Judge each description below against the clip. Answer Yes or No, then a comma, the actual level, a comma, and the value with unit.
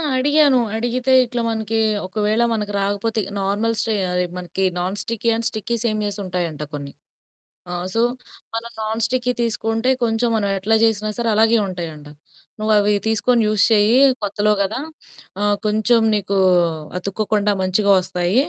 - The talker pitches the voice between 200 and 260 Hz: Yes, high, 215 Hz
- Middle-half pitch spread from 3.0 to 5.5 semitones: No, narrow, 2.5 semitones